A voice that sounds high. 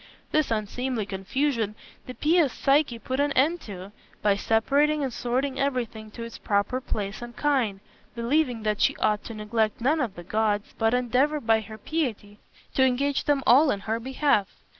Yes: high, 240 Hz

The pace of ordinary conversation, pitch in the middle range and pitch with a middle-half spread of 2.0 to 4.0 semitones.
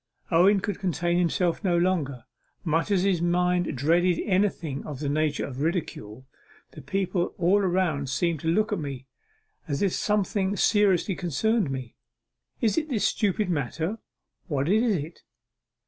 No: average, 150 wpm; medium, 175 Hz; average, 4.4 semitones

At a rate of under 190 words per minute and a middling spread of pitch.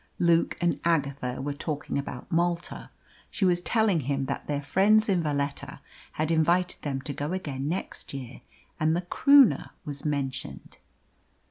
Yes: average, 150 wpm; average, 3.8 semitones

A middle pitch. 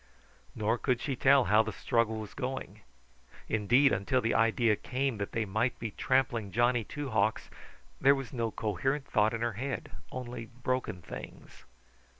No: low, 115 Hz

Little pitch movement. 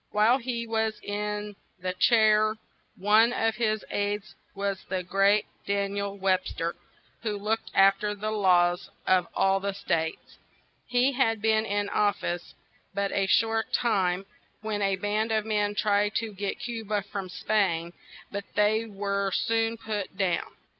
Yes: narrow, 1.8 semitones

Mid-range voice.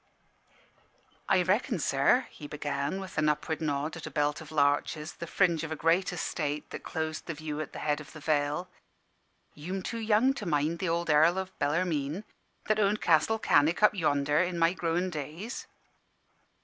Yes: medium, 160 Hz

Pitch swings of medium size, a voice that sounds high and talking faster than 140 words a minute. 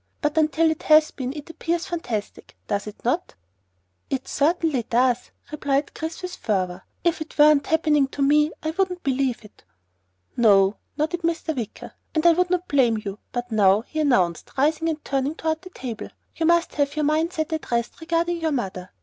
Yes: average, 5.0 semitones; very high, 300 Hz; average, 185 wpm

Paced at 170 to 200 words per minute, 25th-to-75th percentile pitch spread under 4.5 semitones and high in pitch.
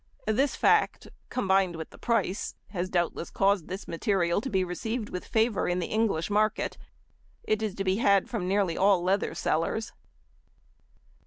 No: average, 160 wpm; average, 3.1 semitones; high, 195 Hz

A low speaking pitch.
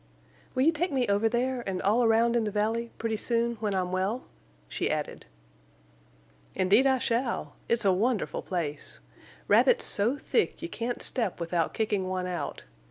No: high, 225 Hz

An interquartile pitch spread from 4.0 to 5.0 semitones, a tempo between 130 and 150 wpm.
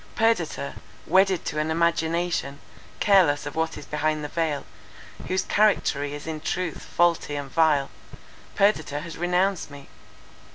No: average, 3.4 semitones; slow, 135 wpm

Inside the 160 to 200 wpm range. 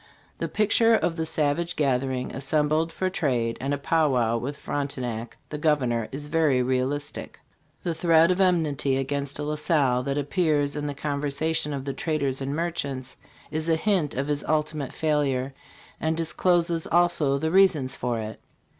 Yes: average, 165 wpm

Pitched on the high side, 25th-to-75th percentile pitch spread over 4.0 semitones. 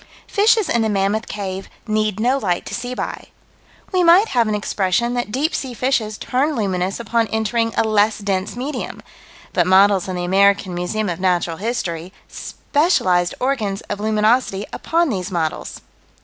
Yes: high, 215 Hz; average, 4.4 semitones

